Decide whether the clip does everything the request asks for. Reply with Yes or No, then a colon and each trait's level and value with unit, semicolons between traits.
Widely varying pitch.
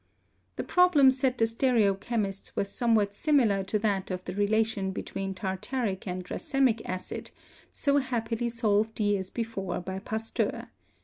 No: average, 3.7 semitones